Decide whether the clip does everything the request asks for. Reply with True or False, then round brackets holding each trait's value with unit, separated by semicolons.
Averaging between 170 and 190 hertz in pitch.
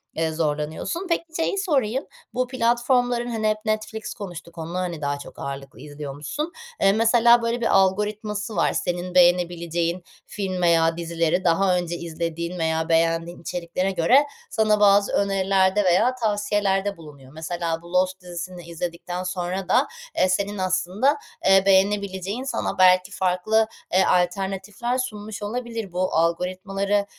True (185 Hz)